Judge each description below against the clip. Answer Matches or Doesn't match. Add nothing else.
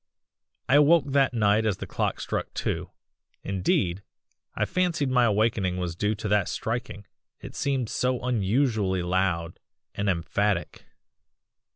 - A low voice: Matches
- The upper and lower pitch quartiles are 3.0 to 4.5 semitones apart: Doesn't match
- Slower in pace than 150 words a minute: Matches